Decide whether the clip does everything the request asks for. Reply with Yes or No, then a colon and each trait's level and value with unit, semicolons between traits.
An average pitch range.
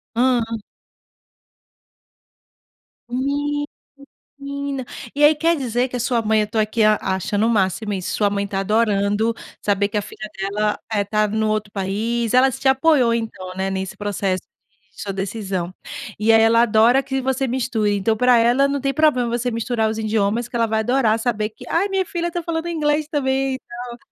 Yes: average, 4.0 semitones